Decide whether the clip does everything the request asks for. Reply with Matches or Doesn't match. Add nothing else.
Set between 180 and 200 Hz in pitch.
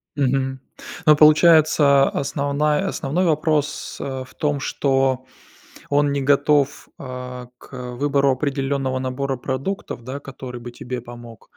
Doesn't match